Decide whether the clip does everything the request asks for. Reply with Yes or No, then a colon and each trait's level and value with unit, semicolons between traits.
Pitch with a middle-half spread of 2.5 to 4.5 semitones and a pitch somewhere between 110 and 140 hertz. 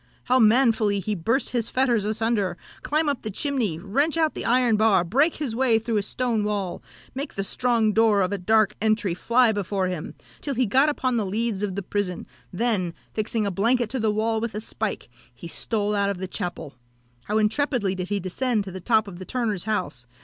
No: average, 3.4 semitones; high, 215 Hz